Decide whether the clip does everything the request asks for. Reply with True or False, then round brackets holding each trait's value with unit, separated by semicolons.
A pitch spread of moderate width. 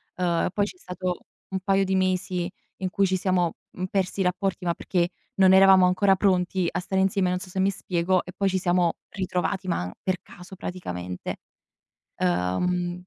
False (1.3 semitones)